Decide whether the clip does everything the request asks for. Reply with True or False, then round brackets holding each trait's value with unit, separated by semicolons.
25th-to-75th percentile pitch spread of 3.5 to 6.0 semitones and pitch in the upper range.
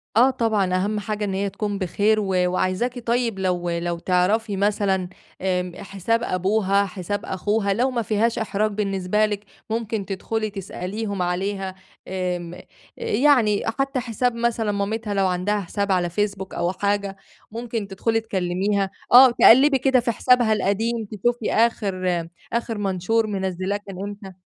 False (2.9 semitones; 205 Hz)